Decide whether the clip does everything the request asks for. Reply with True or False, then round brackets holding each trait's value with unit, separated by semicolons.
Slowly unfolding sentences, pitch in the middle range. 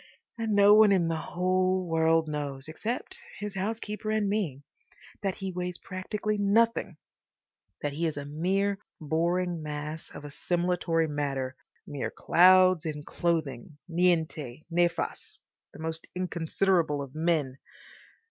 True (120 wpm; 170 Hz)